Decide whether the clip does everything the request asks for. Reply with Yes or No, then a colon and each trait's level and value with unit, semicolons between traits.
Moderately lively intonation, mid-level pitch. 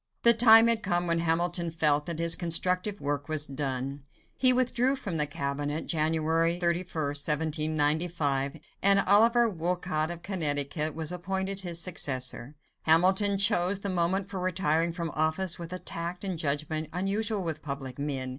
Yes: average, 3.9 semitones; medium, 170 Hz